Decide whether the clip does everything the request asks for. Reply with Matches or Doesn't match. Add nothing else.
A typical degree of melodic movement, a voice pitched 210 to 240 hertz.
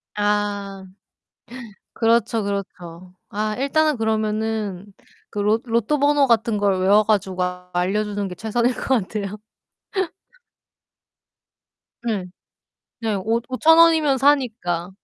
Matches